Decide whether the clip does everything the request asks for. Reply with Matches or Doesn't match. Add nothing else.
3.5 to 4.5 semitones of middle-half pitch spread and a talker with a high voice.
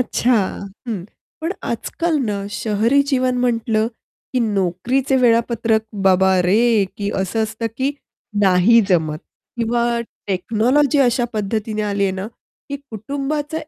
Matches